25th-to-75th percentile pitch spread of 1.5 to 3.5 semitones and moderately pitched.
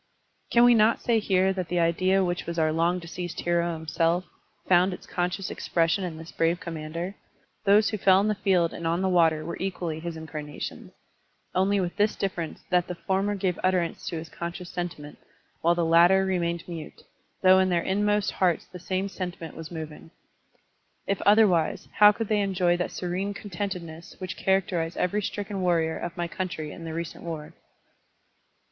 Yes: narrow, 2.4 semitones; medium, 175 Hz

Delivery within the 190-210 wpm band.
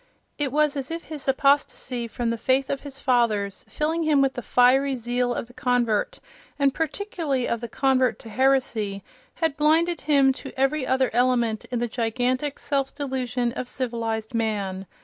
No: average, 170 wpm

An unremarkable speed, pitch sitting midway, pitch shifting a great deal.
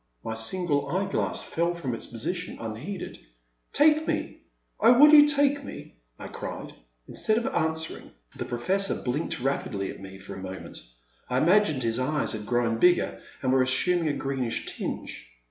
Yes: average, 170 wpm; medium, 145 Hz; wide, 8.2 semitones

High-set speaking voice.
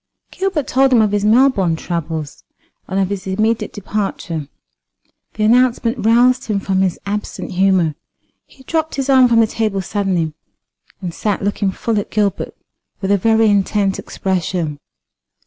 Yes: high, 205 Hz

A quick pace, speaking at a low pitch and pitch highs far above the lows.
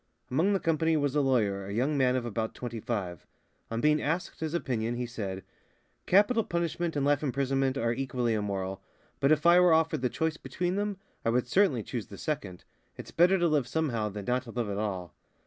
Yes: fast, 210 wpm; low, 130 Hz; wide, 6.0 semitones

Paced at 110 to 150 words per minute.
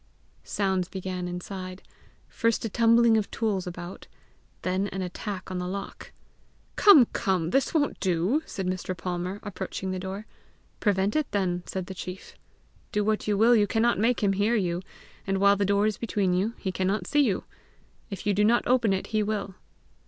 No: average, 180 wpm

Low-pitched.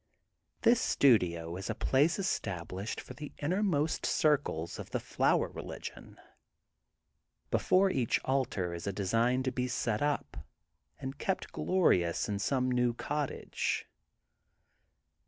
Yes: low, 125 Hz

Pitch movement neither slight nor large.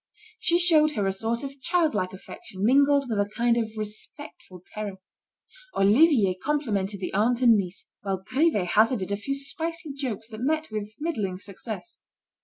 No: wide, 6.1 semitones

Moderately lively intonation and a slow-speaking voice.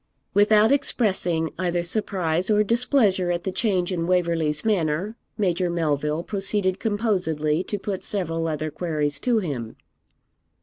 Yes: average, 4.1 semitones; slow, 130 wpm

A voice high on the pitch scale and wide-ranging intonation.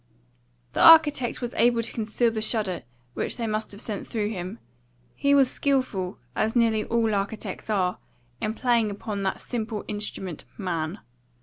No: high, 220 Hz; average, 2.8 semitones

